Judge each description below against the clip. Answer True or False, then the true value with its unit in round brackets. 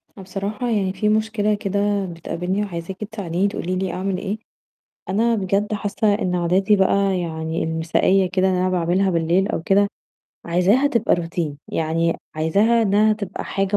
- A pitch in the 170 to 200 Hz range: True (190 Hz)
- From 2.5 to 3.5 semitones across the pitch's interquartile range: True (2.8 semitones)